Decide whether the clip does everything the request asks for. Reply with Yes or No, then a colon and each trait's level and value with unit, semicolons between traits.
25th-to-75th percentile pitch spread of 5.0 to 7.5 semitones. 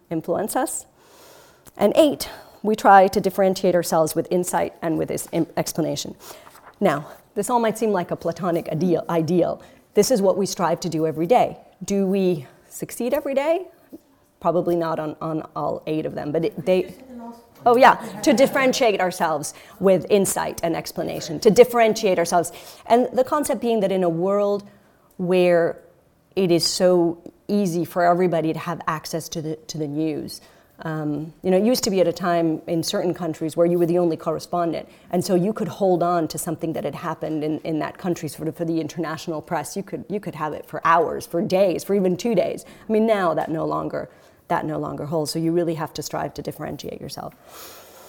No: average, 3.9 semitones